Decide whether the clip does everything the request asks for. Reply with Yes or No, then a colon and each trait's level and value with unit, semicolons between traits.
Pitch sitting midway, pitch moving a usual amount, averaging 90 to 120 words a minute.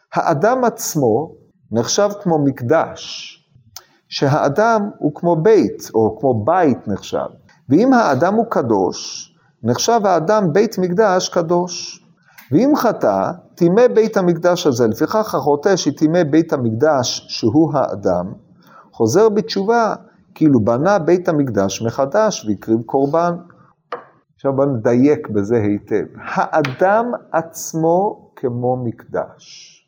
No: medium, 165 Hz; wide, 6.4 semitones; average, 105 wpm